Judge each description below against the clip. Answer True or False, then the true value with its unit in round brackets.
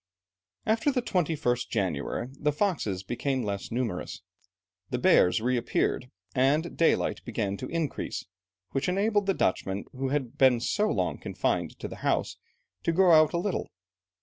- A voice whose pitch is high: False (135 Hz)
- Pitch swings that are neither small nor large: False (6.5 semitones)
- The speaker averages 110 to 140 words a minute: False (150 wpm)